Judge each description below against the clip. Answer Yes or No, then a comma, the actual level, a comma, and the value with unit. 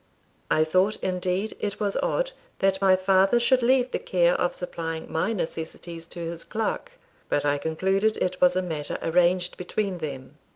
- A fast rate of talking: No, average, 170 wpm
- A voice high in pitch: No, medium, 180 Hz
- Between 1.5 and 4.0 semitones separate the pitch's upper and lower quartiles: Yes, average, 3.2 semitones